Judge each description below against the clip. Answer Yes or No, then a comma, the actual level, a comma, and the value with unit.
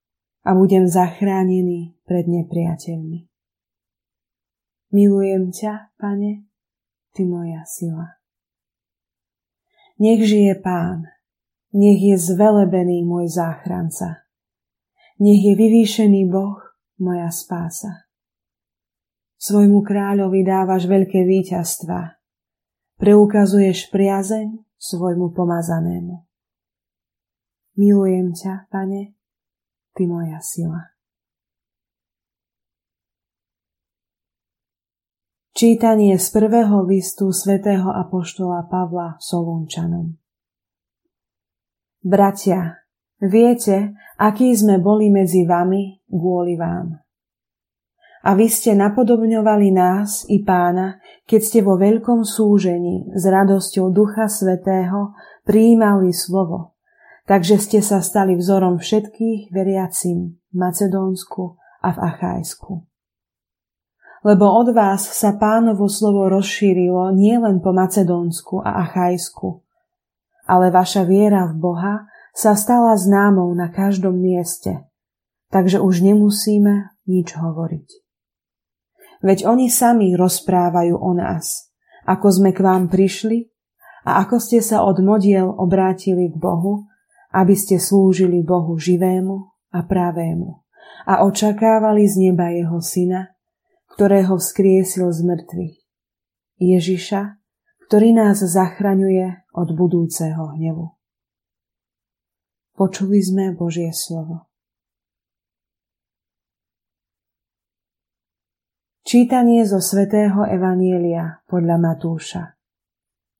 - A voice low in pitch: No, high, 190 Hz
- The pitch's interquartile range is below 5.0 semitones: Yes, average, 2.7 semitones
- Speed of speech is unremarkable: No, slow, 90 wpm